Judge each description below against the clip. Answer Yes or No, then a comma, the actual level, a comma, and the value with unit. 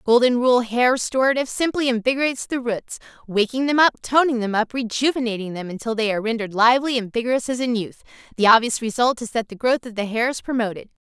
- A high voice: Yes, high, 240 Hz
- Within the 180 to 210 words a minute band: Yes, average, 190 wpm